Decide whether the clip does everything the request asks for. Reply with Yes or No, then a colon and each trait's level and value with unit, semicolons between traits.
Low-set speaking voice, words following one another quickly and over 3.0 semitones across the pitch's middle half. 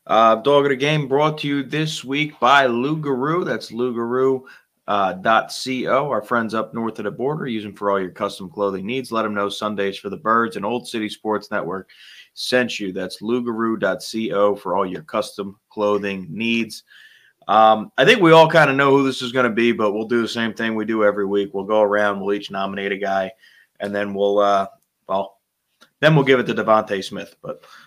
Yes: low, 110 Hz; fast, 210 wpm; average, 4.0 semitones